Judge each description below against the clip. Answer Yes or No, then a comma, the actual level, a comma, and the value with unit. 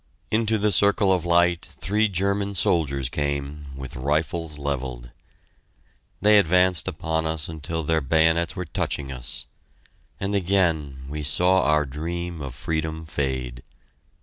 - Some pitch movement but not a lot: Yes, average, 4.2 semitones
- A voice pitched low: Yes, very low, 80 Hz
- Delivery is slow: Yes, slow, 130 wpm